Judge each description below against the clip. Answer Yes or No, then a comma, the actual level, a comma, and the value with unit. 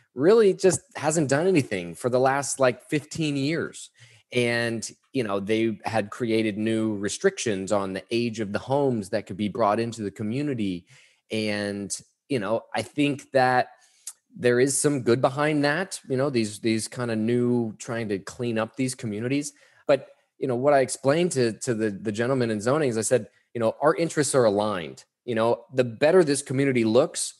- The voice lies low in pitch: Yes, low, 120 Hz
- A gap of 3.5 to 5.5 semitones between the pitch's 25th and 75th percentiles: Yes, average, 4.1 semitones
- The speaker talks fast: No, average, 190 wpm